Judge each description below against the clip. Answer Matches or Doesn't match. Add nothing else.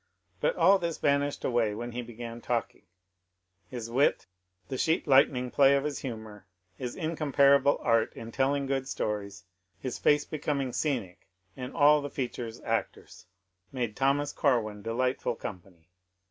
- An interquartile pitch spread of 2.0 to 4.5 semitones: Matches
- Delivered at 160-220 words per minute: Doesn't match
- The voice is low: Matches